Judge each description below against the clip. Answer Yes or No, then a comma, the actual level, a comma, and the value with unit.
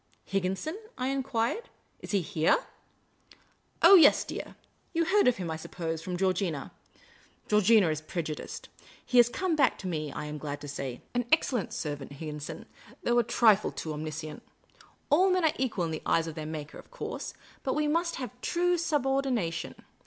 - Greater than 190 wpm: Yes, average, 200 wpm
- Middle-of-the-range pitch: No, high, 195 Hz